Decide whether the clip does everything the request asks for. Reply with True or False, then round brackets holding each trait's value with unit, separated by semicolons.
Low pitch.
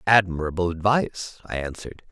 True (95 Hz)